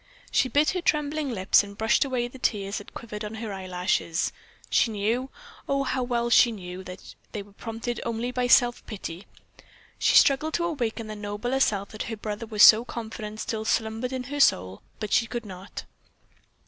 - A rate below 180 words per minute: No, average, 185 wpm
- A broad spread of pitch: No, average, 3.3 semitones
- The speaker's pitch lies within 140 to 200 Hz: No, high, 225 Hz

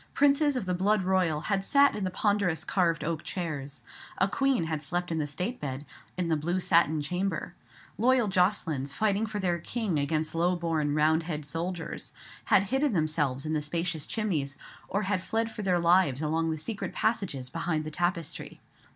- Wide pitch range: No, average, 4.3 semitones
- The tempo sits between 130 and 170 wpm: No, average, 180 wpm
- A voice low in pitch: No, medium, 175 Hz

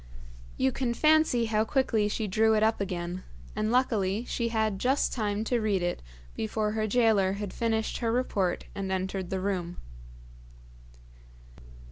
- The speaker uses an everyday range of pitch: Yes, average, 3.2 semitones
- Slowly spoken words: No, average, 150 wpm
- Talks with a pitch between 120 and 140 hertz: No, high, 215 Hz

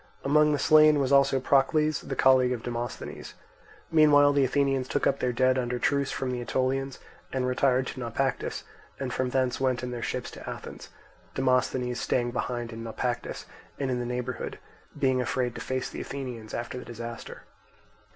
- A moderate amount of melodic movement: No, narrow, 1.8 semitones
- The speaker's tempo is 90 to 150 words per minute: No, average, 175 wpm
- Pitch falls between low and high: No, low, 130 Hz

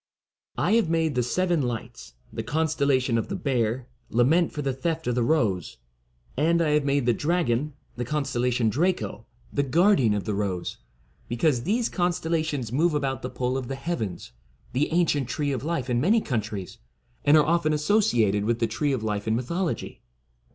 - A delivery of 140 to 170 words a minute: No, average, 185 wpm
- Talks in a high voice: No, medium, 140 Hz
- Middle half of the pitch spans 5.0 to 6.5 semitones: Yes, wide, 5.4 semitones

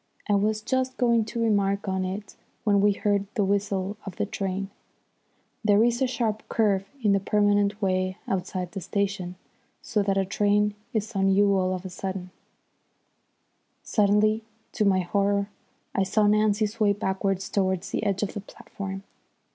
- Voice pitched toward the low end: No, high, 200 Hz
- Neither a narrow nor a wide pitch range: No, narrow, 1.6 semitones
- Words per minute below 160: No, average, 165 wpm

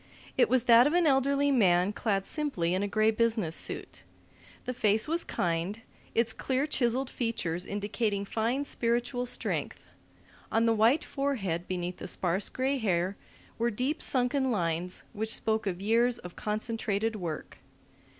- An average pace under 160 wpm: Yes, average, 150 wpm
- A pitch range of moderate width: Yes, average, 4.4 semitones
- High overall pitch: Yes, high, 225 Hz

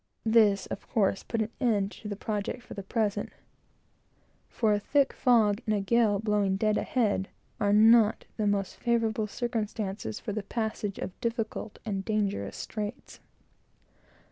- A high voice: Yes, high, 215 Hz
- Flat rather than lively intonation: Yes, narrow, 2.0 semitones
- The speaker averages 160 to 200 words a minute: No, average, 150 wpm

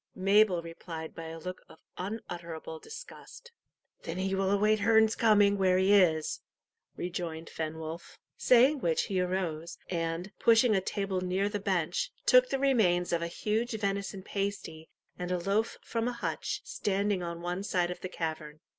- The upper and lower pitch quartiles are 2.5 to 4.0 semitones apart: Yes, average, 3.6 semitones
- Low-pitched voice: No, high, 190 Hz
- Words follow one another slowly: No, average, 165 wpm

